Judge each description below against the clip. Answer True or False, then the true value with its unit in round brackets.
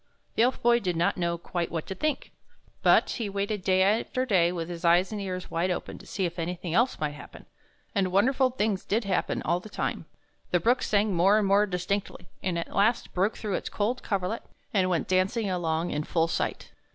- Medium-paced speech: False (215 wpm)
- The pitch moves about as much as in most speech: True (3.3 semitones)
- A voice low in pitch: False (190 Hz)